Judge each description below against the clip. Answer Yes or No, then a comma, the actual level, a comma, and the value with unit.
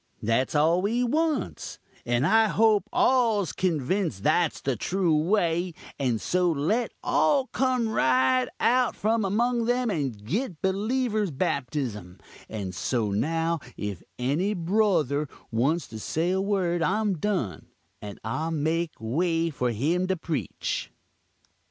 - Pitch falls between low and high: Yes, medium, 170 Hz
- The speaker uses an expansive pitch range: Yes, wide, 7.9 semitones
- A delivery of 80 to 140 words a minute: Yes, slow, 135 wpm